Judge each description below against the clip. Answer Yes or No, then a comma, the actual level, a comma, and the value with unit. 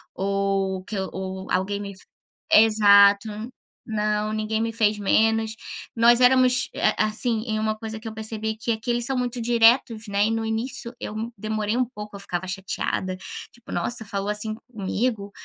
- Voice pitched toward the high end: Yes, high, 220 Hz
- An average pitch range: No, narrow, 2.2 semitones